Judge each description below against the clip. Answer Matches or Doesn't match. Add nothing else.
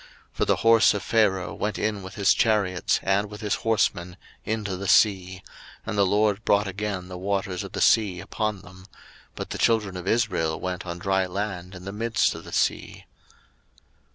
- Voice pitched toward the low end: Matches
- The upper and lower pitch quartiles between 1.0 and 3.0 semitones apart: Matches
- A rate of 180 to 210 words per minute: Matches